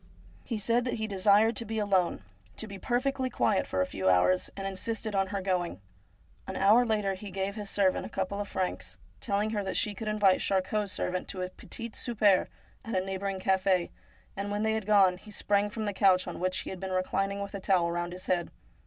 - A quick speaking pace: Yes, fast, 225 wpm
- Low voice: No, high, 195 Hz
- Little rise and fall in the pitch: Yes, narrow, 2.3 semitones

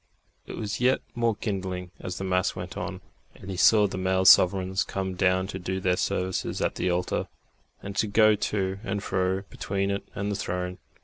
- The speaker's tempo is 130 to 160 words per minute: No, average, 195 wpm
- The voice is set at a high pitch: No, very low, 95 Hz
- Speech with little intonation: Yes, narrow, 1.5 semitones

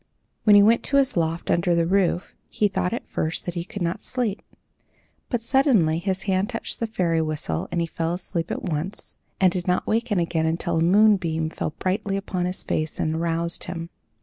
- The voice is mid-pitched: Yes, medium, 180 Hz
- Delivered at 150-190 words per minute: No, average, 200 wpm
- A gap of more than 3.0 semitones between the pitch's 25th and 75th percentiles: Yes, average, 3.5 semitones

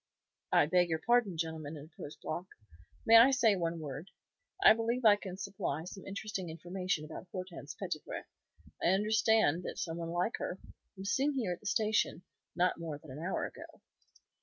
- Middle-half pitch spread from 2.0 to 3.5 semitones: No, average, 4.6 semitones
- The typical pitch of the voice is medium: Yes, medium, 180 Hz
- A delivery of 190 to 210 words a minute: No, average, 175 wpm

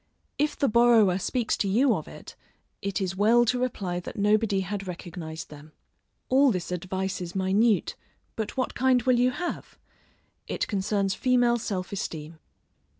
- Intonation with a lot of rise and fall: No, average, 4.5 semitones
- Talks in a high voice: Yes, high, 205 Hz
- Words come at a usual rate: Yes, average, 155 wpm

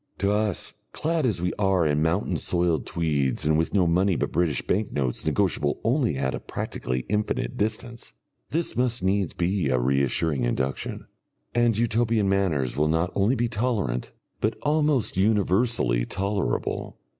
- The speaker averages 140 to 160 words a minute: Yes, average, 155 wpm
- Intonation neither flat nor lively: No, wide, 6.3 semitones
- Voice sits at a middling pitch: No, very low, 95 Hz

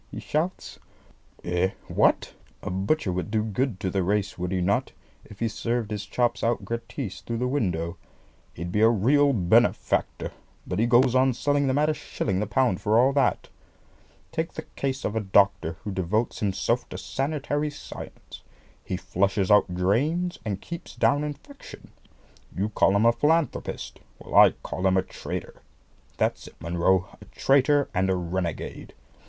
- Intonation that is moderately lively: No, wide, 6.2 semitones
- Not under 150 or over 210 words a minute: Yes, average, 170 wpm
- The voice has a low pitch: Yes, low, 110 Hz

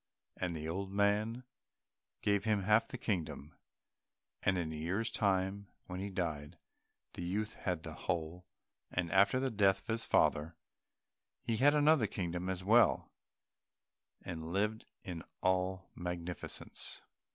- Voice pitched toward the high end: No, very low, 95 Hz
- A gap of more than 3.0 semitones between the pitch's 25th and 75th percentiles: Yes, average, 3.4 semitones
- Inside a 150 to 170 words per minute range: No, average, 140 wpm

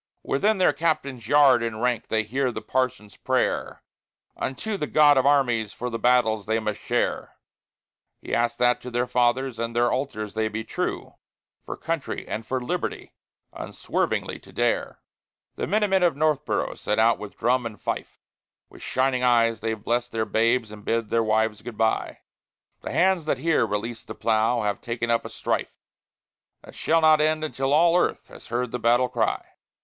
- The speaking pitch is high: No, low, 120 Hz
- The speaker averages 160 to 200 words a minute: Yes, average, 180 wpm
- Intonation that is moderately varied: Yes, average, 3.9 semitones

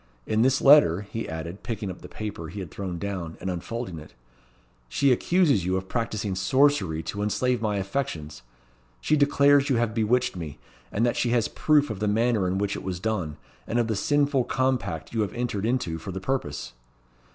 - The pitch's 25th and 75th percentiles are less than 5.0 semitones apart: No, average, 5.3 semitones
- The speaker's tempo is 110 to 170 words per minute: No, average, 195 wpm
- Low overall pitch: Yes, low, 105 Hz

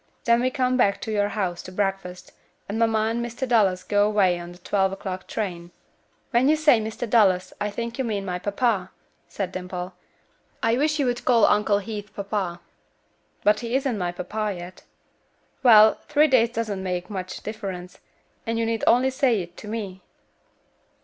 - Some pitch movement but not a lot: Yes, average, 3.8 semitones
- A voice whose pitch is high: Yes, high, 210 Hz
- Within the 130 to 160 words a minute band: No, average, 180 wpm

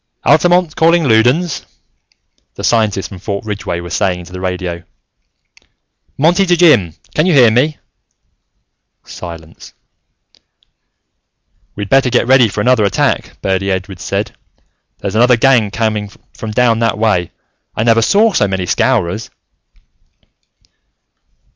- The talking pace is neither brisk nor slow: No, slow, 125 wpm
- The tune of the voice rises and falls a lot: Yes, wide, 5.7 semitones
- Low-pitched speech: Yes, low, 110 Hz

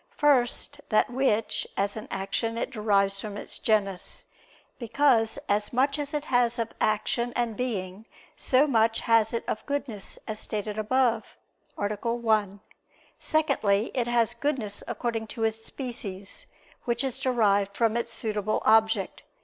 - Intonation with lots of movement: No, average, 2.7 semitones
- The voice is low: No, high, 225 Hz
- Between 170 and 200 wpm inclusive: No, average, 145 wpm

